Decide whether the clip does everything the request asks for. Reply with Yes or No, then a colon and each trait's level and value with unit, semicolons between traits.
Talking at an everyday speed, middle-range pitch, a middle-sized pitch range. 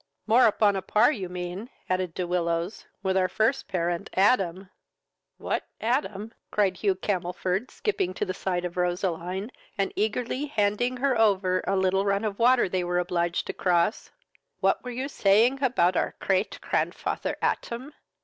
No: average, 160 wpm; high, 195 Hz; average, 3.8 semitones